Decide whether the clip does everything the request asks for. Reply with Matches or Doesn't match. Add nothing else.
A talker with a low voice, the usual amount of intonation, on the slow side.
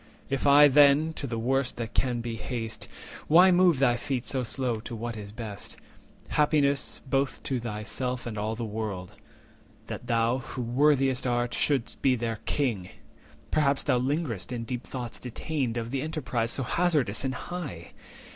Doesn't match